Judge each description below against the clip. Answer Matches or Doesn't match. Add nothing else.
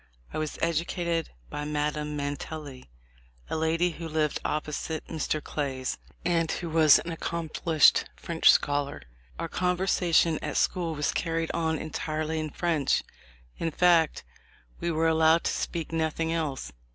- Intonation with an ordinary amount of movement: Doesn't match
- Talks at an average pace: Matches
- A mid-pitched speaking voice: Matches